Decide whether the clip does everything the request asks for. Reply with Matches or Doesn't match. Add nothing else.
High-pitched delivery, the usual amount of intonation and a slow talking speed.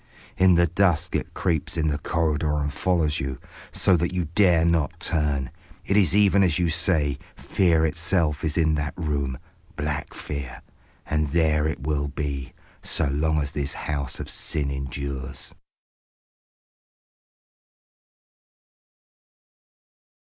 Doesn't match